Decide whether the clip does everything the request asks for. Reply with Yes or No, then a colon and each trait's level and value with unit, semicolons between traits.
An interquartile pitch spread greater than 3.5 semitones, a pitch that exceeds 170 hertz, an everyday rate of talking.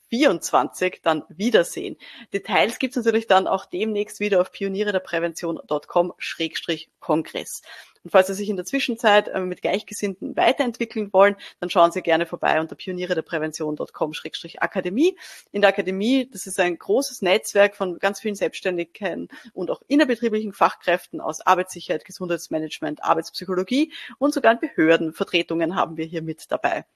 Yes: average, 4.1 semitones; high, 190 Hz; average, 140 wpm